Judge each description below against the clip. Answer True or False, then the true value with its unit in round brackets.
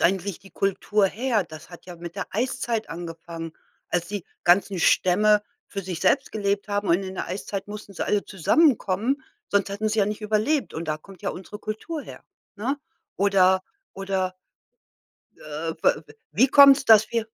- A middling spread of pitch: True (3.1 semitones)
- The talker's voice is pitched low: False (200 Hz)